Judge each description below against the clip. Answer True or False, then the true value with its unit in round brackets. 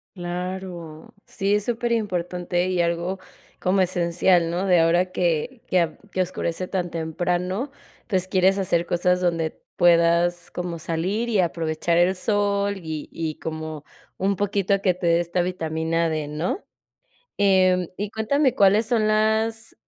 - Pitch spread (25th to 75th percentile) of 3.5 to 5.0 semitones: False (2.5 semitones)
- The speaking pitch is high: False (180 Hz)